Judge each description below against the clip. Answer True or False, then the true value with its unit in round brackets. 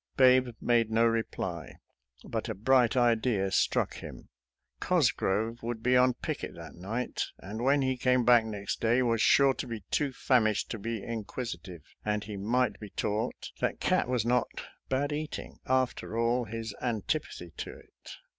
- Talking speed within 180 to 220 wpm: False (165 wpm)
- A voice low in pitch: True (115 Hz)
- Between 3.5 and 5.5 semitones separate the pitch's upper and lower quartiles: False (2.9 semitones)